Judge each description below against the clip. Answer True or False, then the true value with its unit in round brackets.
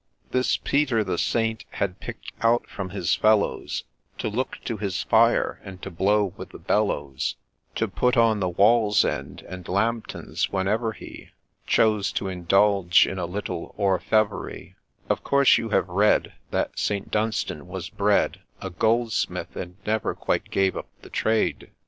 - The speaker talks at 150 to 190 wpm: True (160 wpm)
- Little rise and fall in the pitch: False (3.1 semitones)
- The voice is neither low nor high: False (100 Hz)